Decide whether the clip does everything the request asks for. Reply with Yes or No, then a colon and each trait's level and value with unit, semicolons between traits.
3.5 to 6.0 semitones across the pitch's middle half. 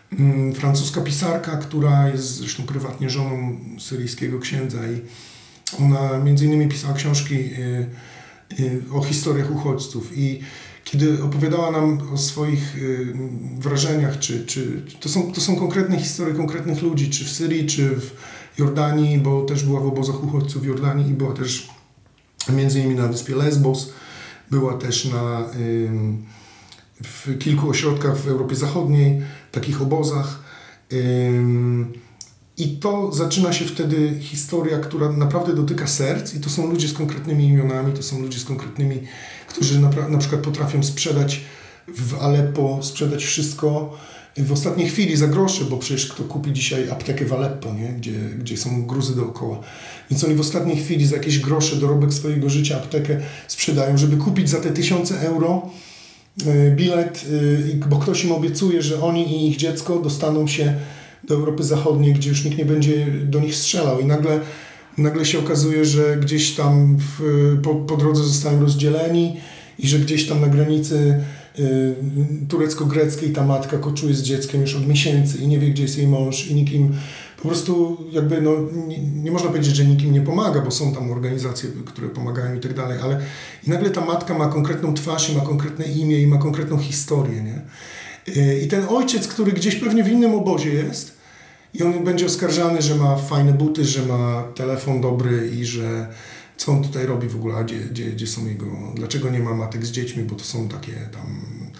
No: narrow, 2.5 semitones